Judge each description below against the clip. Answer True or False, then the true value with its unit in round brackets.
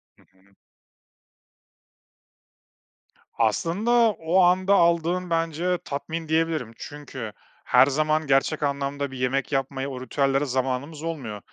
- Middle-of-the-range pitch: True (145 Hz)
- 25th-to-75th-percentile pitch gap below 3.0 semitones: False (3.7 semitones)